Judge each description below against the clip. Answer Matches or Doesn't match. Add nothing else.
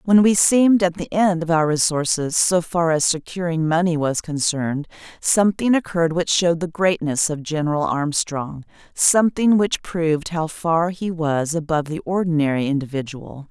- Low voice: Doesn't match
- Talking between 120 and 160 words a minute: Matches